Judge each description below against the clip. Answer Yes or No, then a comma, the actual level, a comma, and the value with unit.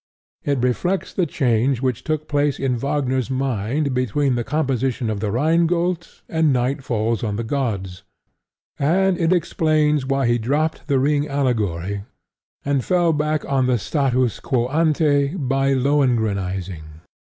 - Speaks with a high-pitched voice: No, low, 135 Hz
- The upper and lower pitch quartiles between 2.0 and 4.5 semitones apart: Yes, average, 4.1 semitones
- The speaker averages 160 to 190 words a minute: No, average, 145 wpm